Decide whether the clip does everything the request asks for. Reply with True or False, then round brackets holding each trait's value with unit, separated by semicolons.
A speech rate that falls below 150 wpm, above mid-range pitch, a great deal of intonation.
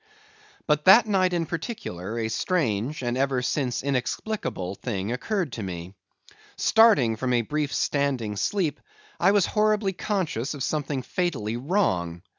False (140 wpm; 140 Hz; 8.3 semitones)